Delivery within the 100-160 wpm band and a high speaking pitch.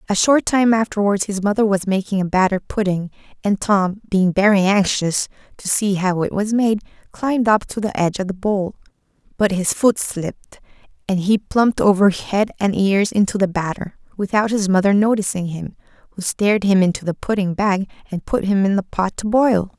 No: average, 195 wpm; high, 200 Hz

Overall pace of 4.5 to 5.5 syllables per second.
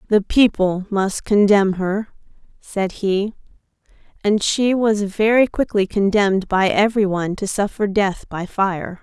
No: 4.1 syllables/s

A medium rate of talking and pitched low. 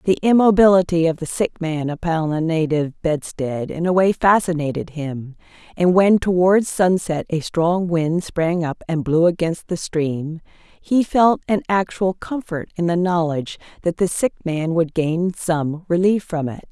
No: average, 170 wpm; medium, 170 Hz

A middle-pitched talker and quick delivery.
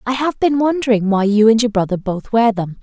No: high, 225 Hz; fast, 255 wpm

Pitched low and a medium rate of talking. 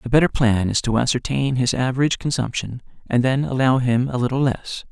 Yes: low, 130 Hz; average, 195 wpm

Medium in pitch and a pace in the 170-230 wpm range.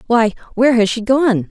No: high, 230 Hz; average, 200 wpm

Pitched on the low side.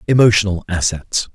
Yes: low, 100 Hz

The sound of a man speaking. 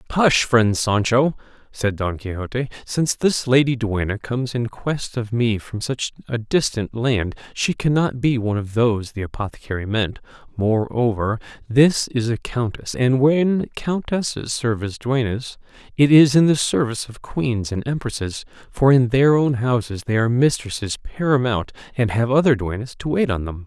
Yes: male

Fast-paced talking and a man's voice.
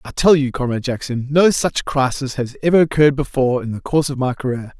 Yes: fast, 225 wpm; male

